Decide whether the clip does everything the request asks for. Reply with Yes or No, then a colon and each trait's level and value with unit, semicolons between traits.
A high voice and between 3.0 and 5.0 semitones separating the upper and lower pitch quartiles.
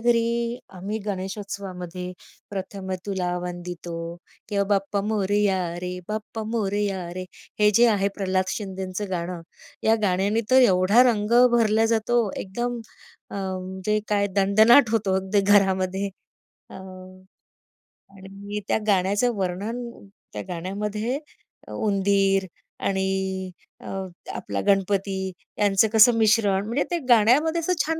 No: high, 200 Hz; narrow, 2.5 semitones